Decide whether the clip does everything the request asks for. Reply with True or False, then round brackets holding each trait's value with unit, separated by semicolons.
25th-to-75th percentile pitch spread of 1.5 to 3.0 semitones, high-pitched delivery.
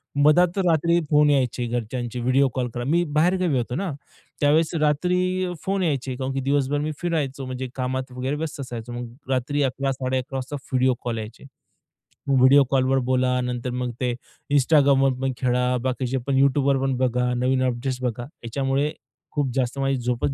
False (2.5 semitones; 135 Hz)